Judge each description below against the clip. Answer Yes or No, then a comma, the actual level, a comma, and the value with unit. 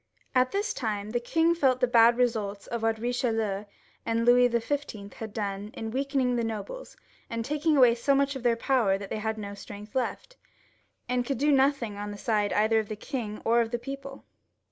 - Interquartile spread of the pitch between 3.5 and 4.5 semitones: Yes, average, 3.8 semitones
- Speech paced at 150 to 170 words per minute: No, fast, 205 wpm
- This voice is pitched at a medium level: No, high, 235 Hz